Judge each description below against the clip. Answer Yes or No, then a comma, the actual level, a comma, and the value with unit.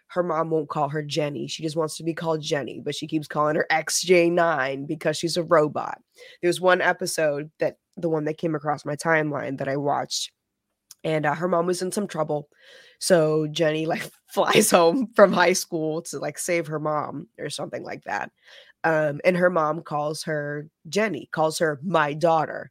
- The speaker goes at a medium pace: Yes, average, 195 wpm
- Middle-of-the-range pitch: Yes, medium, 160 Hz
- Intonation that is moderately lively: No, narrow, 2.3 semitones